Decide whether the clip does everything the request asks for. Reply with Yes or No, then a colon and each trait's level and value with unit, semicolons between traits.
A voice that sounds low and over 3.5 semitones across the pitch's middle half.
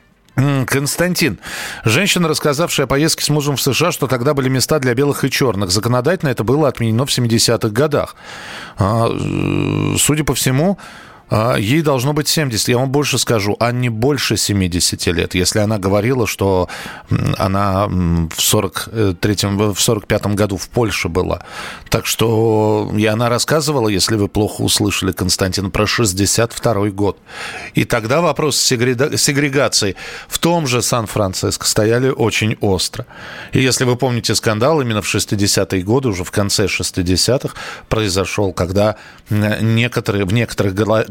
Yes: low, 115 Hz; average, 5.1 semitones